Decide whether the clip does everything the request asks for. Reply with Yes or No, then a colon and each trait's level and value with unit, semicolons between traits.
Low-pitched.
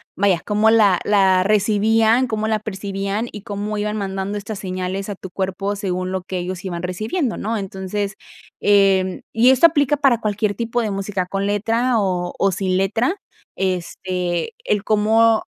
No: high, 200 Hz